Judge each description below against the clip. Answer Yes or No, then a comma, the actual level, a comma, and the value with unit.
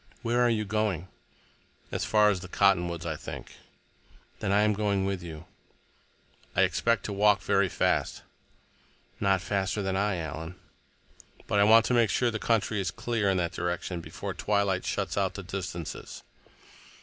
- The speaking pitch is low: Yes, low, 100 Hz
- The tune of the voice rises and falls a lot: No, average, 2.8 semitones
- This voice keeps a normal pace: Yes, average, 165 wpm